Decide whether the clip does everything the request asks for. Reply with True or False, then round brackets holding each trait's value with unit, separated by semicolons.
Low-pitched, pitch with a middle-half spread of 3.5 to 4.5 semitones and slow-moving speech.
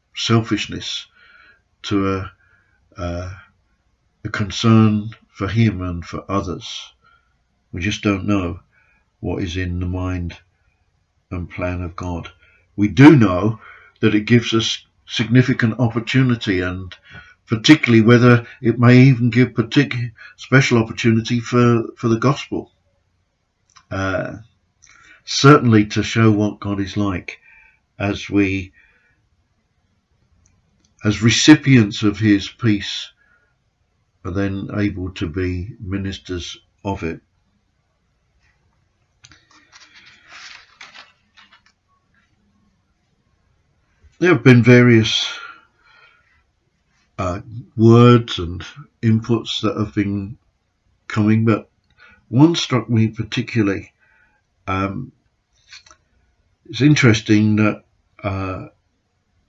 True (105 Hz; 3.8 semitones; 95 wpm)